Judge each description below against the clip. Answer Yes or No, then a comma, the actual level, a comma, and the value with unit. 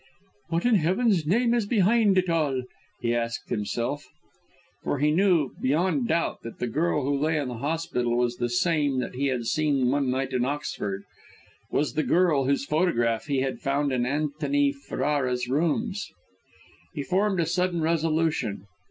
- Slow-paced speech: No, average, 165 wpm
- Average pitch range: Yes, average, 4.7 semitones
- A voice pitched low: No, medium, 145 Hz